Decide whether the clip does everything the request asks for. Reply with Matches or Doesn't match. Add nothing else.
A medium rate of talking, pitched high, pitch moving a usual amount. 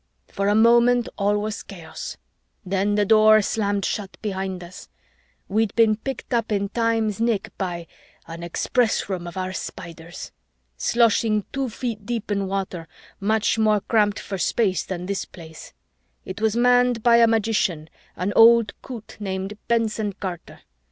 Matches